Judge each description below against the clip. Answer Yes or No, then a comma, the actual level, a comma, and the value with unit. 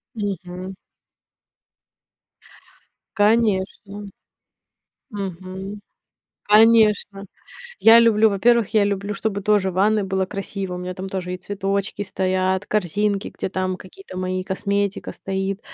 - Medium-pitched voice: No, high, 195 Hz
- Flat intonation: Yes, narrow, 1.8 semitones